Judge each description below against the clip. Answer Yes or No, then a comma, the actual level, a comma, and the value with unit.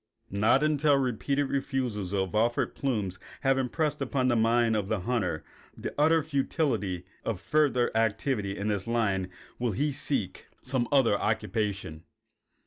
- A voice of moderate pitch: No, low, 115 Hz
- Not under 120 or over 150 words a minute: Yes, average, 140 wpm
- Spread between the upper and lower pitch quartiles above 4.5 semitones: Yes, average, 5.0 semitones